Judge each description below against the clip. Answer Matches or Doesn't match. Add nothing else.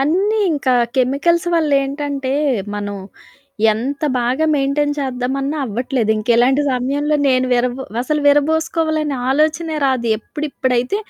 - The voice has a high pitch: Matches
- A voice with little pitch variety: Doesn't match